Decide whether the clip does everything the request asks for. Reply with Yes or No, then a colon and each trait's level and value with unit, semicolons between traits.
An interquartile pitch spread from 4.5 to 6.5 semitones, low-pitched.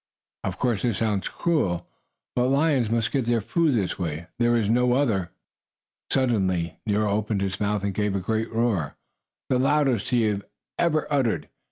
No: average, 4.1 semitones; low, 110 Hz